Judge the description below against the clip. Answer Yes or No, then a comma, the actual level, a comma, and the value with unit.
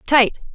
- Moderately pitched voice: No, very high, 255 Hz